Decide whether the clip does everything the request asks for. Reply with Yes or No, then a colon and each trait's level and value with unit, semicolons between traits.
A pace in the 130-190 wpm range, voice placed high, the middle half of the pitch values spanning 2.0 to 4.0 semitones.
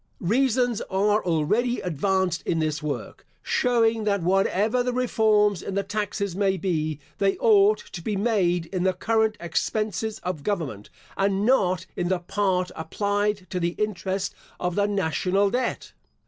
Yes: average, 150 wpm; high, 195 Hz; average, 3.1 semitones